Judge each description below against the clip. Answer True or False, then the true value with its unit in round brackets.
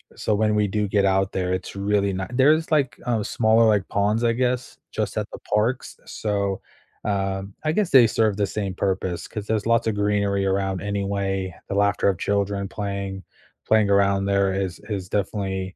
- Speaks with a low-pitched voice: True (100 Hz)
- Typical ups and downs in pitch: False (1.8 semitones)